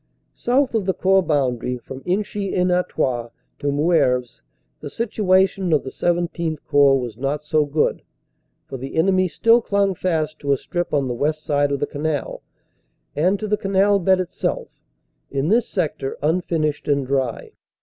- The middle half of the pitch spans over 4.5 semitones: Yes, average, 5.1 semitones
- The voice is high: No, medium, 155 Hz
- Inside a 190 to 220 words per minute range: No, average, 165 wpm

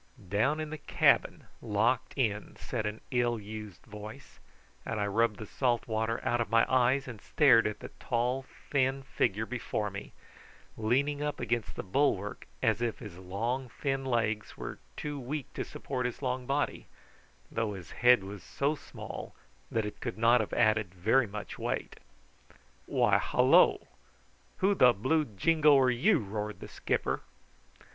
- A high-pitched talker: No, low, 120 Hz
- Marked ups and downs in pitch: No, average, 3.9 semitones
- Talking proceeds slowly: No, average, 160 wpm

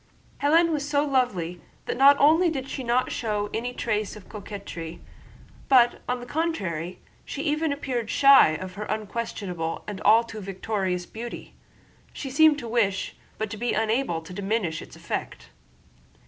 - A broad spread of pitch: Yes, wide, 5.9 semitones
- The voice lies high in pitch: Yes, high, 225 Hz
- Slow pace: No, average, 160 wpm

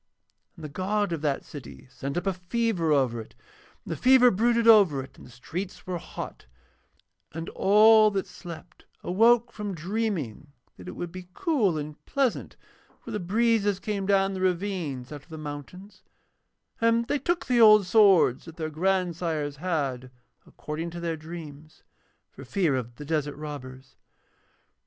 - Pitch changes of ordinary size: No, wide, 5.8 semitones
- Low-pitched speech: No, medium, 175 Hz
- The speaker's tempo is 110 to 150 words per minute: No, average, 165 wpm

